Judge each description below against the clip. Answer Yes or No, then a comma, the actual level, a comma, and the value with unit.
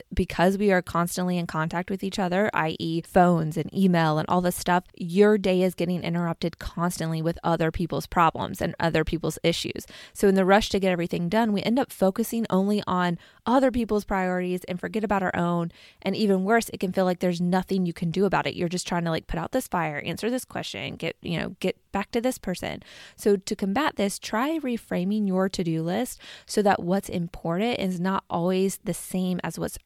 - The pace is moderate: No, fast, 215 wpm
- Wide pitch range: No, average, 2.8 semitones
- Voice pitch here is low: No, medium, 185 Hz